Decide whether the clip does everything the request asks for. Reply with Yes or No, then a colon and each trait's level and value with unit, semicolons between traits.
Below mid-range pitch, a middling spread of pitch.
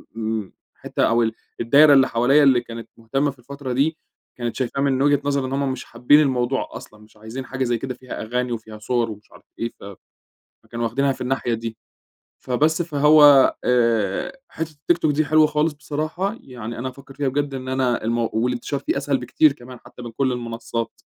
Yes: low, 130 Hz; average, 3.3 semitones